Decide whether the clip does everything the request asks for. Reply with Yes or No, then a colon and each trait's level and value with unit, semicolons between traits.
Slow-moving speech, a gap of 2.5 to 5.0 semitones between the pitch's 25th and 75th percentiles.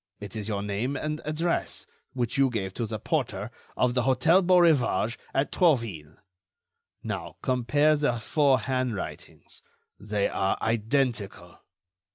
No: slow, 130 wpm; wide, 5.5 semitones